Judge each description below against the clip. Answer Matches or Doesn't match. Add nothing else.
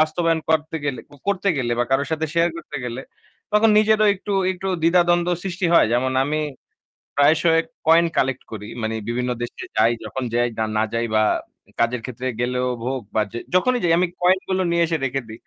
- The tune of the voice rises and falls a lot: Matches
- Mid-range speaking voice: Matches